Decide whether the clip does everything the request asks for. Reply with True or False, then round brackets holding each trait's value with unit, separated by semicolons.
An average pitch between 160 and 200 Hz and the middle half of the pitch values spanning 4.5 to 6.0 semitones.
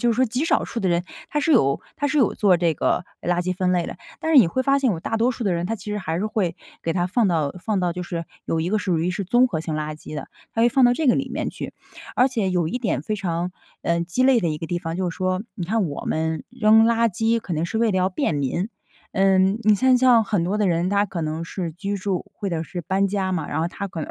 True (190 Hz; 4.9 semitones)